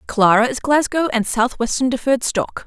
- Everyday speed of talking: Yes, average, 160 wpm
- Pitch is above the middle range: Yes, very high, 250 Hz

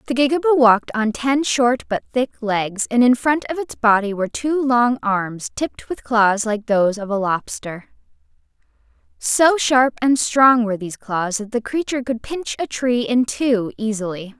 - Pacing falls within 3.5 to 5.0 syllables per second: Yes, 4.6 syllables/s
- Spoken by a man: No, female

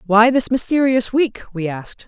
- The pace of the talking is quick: No, average, 175 wpm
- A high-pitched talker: Yes, high, 230 Hz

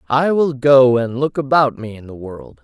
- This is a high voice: No, low, 125 Hz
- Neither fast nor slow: No, fast, 230 wpm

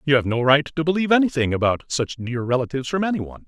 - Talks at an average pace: No, fast, 240 wpm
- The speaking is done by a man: Yes, male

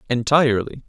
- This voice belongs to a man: Yes, male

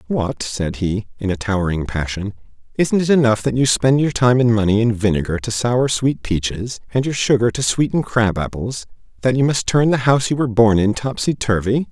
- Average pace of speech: No, fast, 210 wpm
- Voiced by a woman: No, male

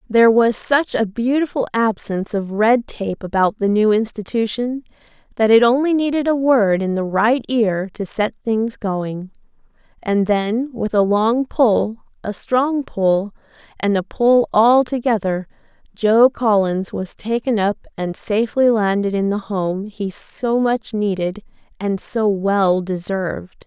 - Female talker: Yes, female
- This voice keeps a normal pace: Yes, average, 150 wpm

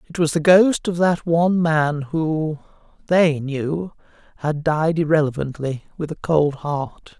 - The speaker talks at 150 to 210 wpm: No, slow, 135 wpm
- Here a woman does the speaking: No, male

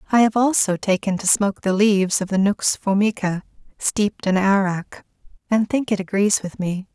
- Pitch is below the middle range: No, high, 200 Hz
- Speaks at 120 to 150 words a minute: No, average, 180 wpm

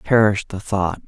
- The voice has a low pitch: Yes, low, 100 Hz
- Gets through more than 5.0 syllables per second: No, 4.2 syllables/s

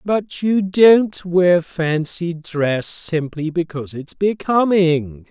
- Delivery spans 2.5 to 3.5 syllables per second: Yes, 3.1 syllables/s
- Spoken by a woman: No, male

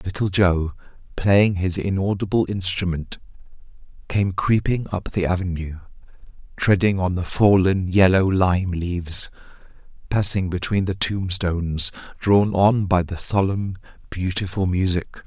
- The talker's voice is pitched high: No, very low, 95 Hz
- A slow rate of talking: Yes, slow, 115 wpm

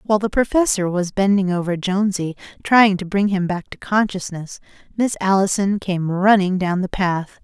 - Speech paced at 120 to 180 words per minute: Yes, average, 170 wpm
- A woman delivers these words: Yes, female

